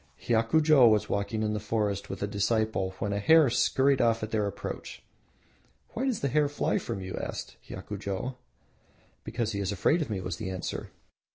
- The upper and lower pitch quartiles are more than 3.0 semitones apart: Yes, average, 3.9 semitones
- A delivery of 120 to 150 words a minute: No, average, 185 wpm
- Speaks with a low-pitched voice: Yes, low, 110 Hz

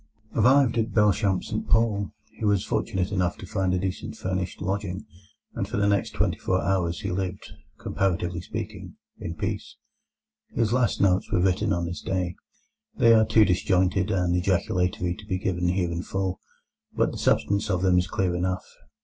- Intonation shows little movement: Yes, narrow, 2.2 semitones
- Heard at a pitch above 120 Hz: No, very low, 95 Hz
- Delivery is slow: No, average, 175 wpm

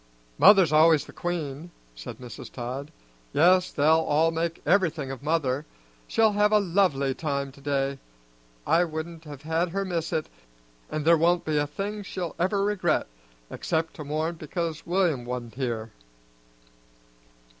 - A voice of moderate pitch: Yes, medium, 160 Hz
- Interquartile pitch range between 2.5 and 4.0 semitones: Yes, average, 3.7 semitones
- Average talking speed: Yes, average, 150 wpm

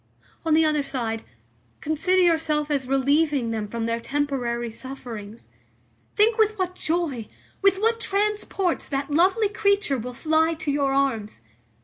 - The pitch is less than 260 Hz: No, very high, 295 Hz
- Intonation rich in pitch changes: Yes, wide, 6.4 semitones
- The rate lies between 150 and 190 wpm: No, average, 140 wpm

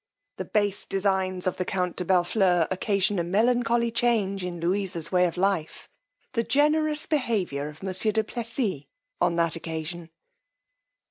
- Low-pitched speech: No, high, 190 Hz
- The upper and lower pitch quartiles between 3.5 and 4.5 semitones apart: Yes, average, 4.2 semitones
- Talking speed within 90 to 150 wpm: Yes, average, 145 wpm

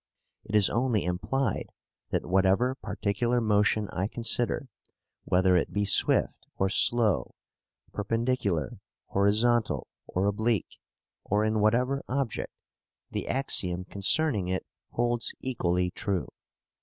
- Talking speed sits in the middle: No, slow, 110 wpm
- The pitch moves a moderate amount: Yes, average, 4.1 semitones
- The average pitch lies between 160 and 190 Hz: No, low, 105 Hz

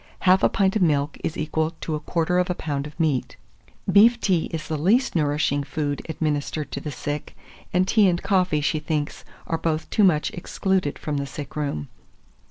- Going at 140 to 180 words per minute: No, average, 195 wpm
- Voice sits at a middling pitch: Yes, medium, 155 Hz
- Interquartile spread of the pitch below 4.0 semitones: Yes, average, 3.6 semitones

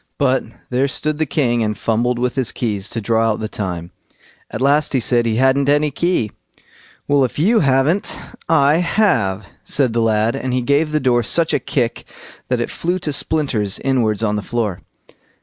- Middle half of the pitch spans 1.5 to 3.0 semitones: No, average, 4.5 semitones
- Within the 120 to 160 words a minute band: No, average, 190 wpm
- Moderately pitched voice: No, low, 125 Hz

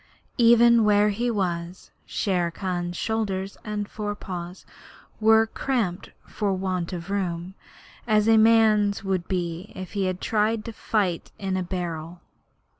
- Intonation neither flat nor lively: Yes, average, 3.3 semitones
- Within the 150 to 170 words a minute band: No, slow, 135 wpm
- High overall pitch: Yes, high, 195 Hz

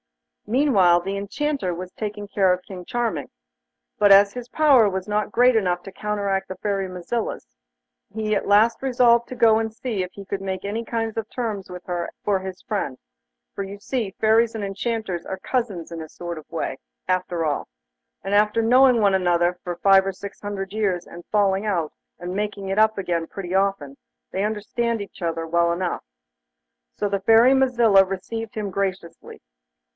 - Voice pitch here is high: Yes, high, 200 Hz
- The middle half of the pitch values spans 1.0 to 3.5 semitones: Yes, average, 3.2 semitones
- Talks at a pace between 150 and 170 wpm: No, average, 185 wpm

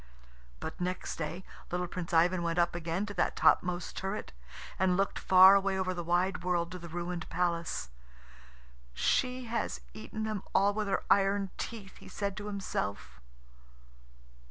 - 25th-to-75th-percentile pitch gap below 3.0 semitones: Yes, narrow, 2.4 semitones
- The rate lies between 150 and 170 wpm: Yes, average, 155 wpm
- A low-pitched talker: No, medium, 180 Hz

